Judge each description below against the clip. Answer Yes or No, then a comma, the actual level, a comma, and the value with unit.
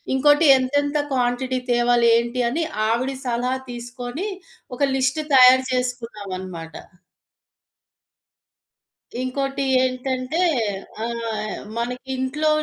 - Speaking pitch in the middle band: No, very high, 255 Hz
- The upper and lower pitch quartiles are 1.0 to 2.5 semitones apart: Yes, narrow, 1.9 semitones